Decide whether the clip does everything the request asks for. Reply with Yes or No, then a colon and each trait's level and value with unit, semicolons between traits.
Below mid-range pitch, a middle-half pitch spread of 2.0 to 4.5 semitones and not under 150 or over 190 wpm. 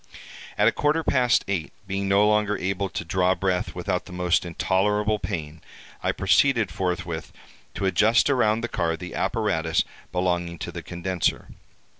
Yes: very low, 95 Hz; average, 3.3 semitones; average, 155 wpm